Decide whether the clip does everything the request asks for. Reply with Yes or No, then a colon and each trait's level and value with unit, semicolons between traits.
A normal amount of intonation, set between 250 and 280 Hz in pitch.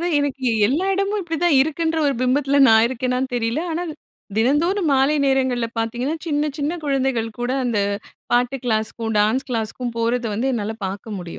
Yes: average, 4.2 semitones; very high, 260 Hz